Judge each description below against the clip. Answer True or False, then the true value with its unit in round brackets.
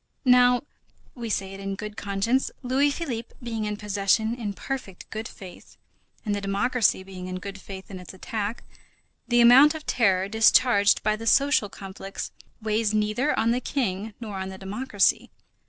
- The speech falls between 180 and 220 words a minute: False (170 wpm)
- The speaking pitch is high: True (215 Hz)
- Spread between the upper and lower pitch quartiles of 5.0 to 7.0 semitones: False (3.7 semitones)